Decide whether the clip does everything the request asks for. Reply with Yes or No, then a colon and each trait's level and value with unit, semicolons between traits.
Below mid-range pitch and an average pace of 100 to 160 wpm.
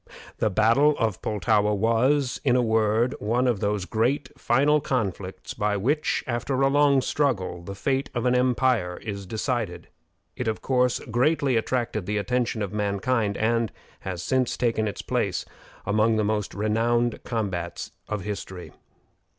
Yes: low, 115 Hz; average, 150 wpm